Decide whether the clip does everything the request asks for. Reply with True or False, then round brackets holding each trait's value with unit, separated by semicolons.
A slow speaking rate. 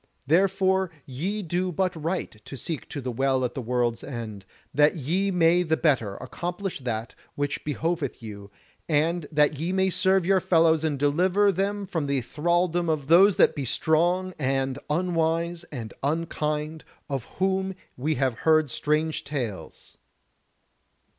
False (150 wpm)